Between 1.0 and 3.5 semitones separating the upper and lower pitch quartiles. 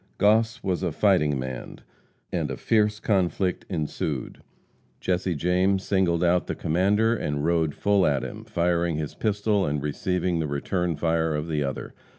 No: average, 4.1 semitones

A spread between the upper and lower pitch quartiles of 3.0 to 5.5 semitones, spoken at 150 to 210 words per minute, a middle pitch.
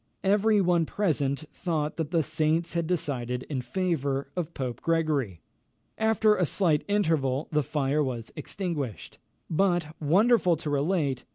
No: average, 4.3 semitones; slow, 135 wpm; medium, 155 Hz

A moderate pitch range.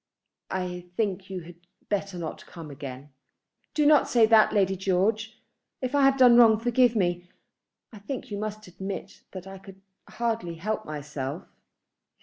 Yes: average, 4.0 semitones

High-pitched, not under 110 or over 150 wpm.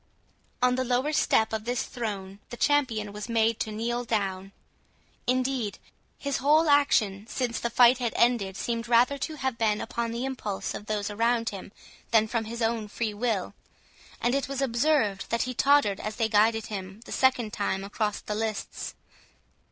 No: high, 230 Hz; average, 175 wpm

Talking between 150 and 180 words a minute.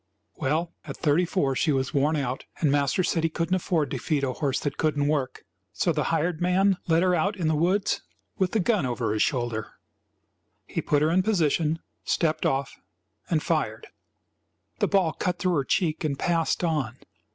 No: average, 190 wpm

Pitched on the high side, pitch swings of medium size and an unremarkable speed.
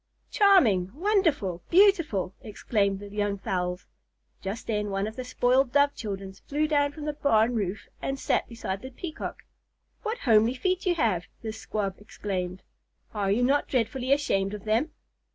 No: high, 225 Hz; wide, 6.4 semitones; average, 160 wpm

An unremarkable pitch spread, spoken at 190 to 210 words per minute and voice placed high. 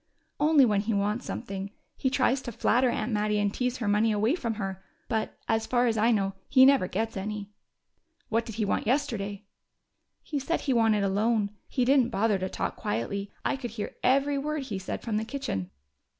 Yes: average, 3.8 semitones; fast, 205 wpm; high, 225 Hz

